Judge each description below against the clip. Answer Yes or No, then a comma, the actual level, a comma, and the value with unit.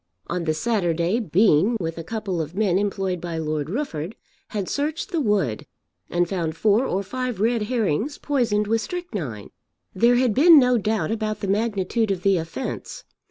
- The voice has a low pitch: No, high, 205 Hz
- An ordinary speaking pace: Yes, average, 170 wpm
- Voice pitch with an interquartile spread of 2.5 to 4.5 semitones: No, average, 5.3 semitones